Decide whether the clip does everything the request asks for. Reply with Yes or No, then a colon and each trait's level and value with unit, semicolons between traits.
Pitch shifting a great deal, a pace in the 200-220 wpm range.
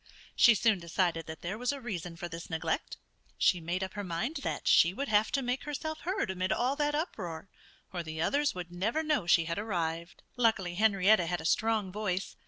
Yes: wide, 5.9 semitones; fast, 205 wpm